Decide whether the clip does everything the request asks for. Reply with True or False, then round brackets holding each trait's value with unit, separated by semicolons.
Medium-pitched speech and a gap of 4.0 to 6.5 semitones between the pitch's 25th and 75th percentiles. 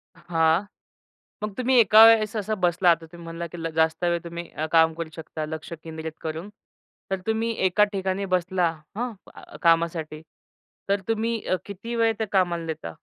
True (175 Hz; 4.4 semitones)